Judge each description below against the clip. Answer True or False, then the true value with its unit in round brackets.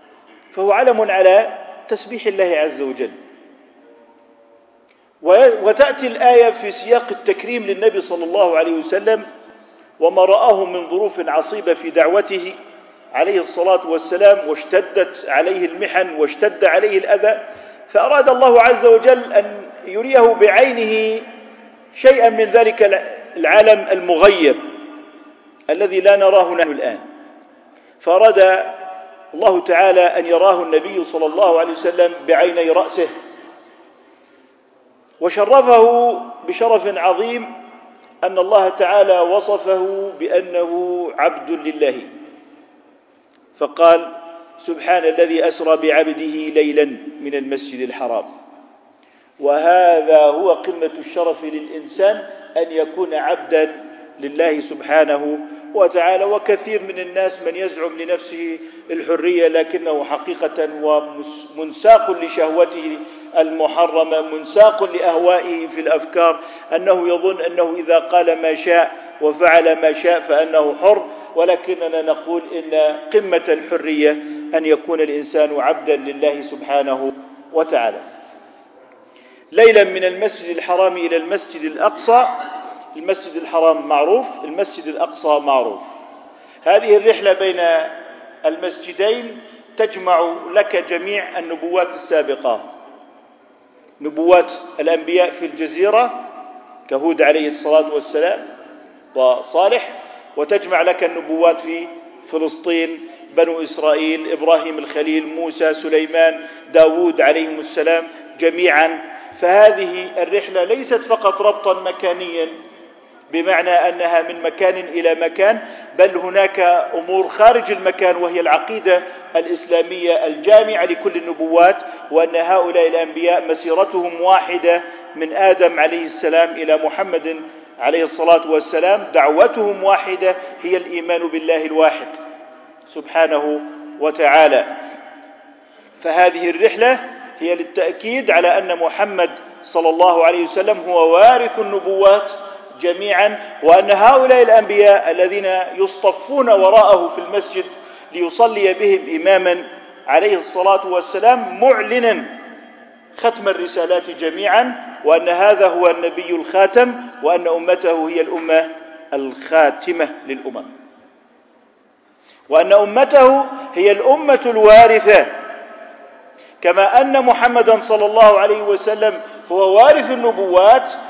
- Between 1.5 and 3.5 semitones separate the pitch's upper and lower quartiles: False (5.5 semitones)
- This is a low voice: False (180 Hz)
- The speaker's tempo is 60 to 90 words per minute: False (100 wpm)